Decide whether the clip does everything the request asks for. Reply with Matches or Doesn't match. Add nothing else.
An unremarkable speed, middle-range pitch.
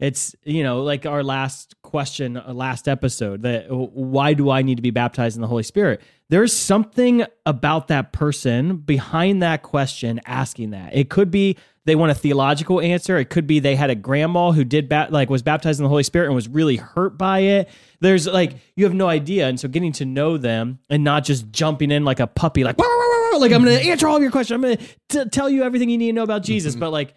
Doesn't match